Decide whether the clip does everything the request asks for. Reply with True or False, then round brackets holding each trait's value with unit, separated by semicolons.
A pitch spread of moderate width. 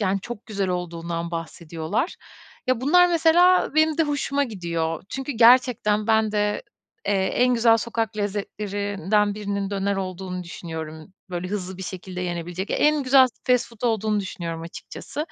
True (4.9 semitones)